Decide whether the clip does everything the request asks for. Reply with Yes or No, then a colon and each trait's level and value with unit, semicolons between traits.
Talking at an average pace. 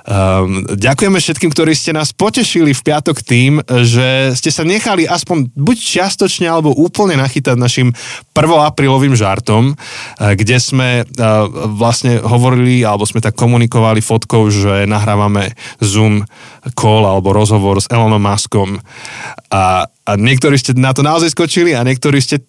Yes: average, 140 wpm